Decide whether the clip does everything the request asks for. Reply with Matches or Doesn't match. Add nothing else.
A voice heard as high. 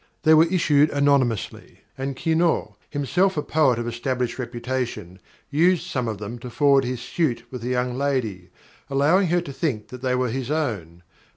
Doesn't match